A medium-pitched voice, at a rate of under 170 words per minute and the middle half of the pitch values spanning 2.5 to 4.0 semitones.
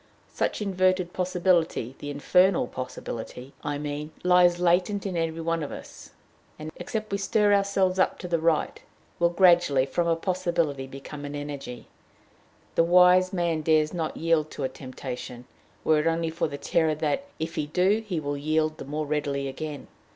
No: medium, 165 Hz; average, 175 wpm; average, 3.7 semitones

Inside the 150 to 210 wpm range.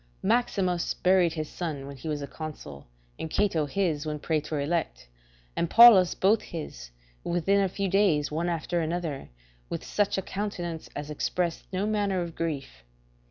Yes: average, 175 wpm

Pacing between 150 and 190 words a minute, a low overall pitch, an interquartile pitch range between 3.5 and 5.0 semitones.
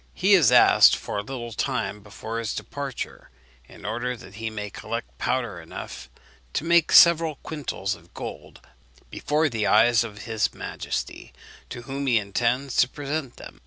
Yes: average, 160 wpm; low, 120 Hz; average, 4.7 semitones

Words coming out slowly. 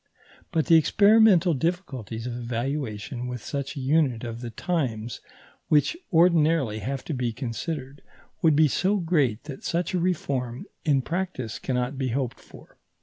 No: average, 150 wpm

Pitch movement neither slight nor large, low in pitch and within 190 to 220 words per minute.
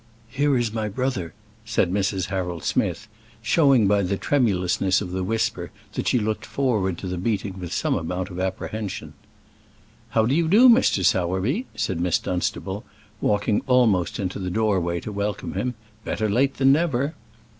No: average, 4.9 semitones; low, 105 Hz; average, 165 wpm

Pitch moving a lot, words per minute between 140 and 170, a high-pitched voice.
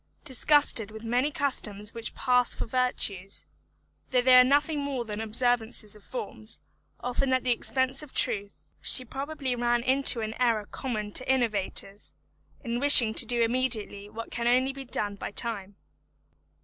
No: average, 3.2 semitones; average, 160 wpm; high, 240 Hz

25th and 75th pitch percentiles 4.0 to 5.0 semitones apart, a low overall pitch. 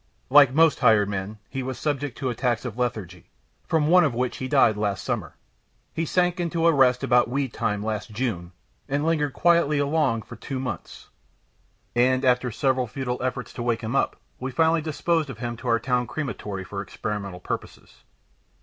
Yes: average, 4.4 semitones; low, 125 Hz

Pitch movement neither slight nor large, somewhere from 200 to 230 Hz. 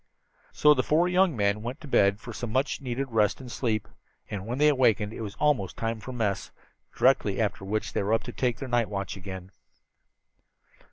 No: average, 4.2 semitones; low, 115 Hz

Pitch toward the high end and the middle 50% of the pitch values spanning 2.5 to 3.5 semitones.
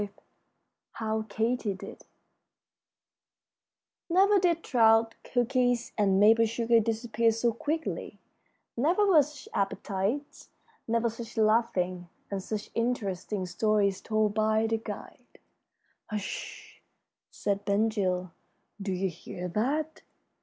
Yes: high, 220 Hz; average, 3.1 semitones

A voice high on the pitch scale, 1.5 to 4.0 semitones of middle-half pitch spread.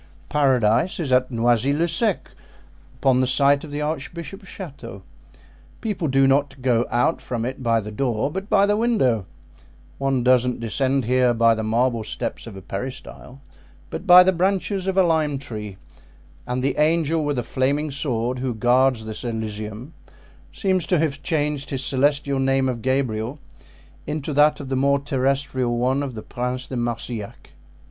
No: low, 135 Hz; average, 3.6 semitones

